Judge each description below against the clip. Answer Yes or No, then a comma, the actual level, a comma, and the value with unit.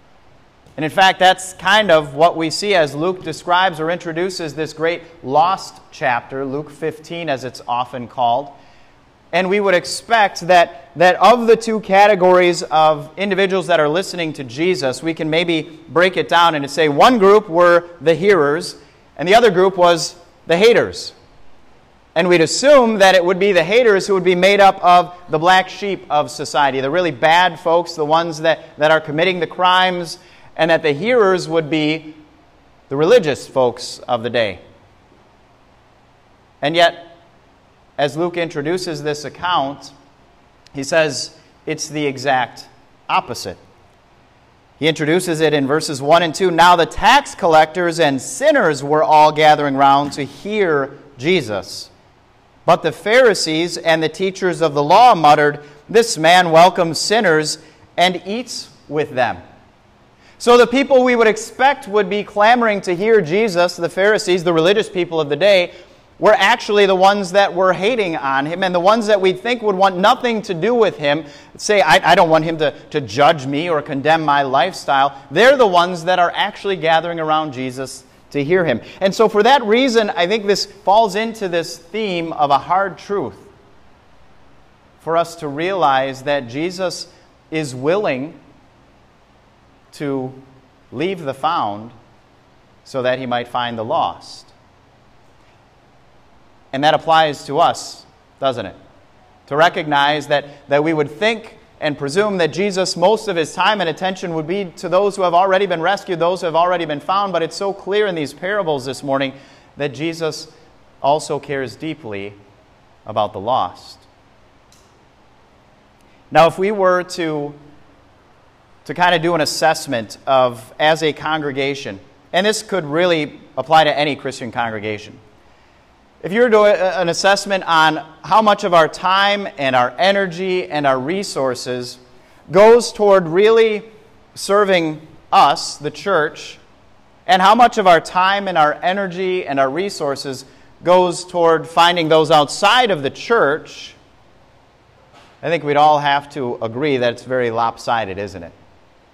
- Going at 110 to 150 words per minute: No, average, 160 wpm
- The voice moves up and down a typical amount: Yes, average, 4.6 semitones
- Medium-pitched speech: Yes, medium, 165 Hz